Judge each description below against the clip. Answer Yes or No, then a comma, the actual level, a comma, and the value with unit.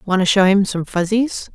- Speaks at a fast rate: Yes, fast, 235 wpm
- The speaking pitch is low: No, high, 195 Hz